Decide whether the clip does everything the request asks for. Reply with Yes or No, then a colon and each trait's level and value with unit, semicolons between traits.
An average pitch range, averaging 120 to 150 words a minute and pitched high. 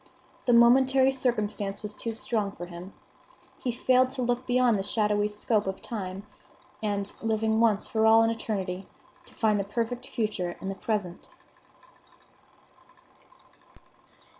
Yes: average, 3.0 semitones; average, 140 wpm; high, 220 Hz